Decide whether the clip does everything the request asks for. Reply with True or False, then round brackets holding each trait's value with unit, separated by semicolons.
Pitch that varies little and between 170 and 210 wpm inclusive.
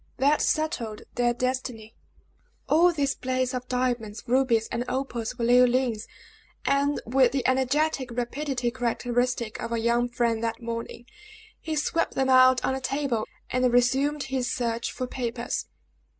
False (2.1 semitones; 145 wpm)